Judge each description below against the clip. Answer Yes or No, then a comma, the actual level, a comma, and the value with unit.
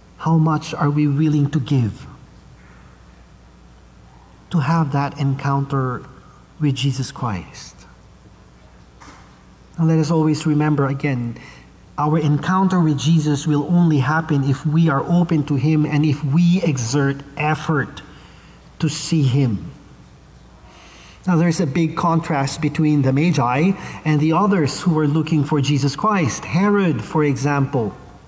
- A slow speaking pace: Yes, slow, 130 wpm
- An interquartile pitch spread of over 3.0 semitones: No, average, 2.7 semitones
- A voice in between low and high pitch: Yes, medium, 150 Hz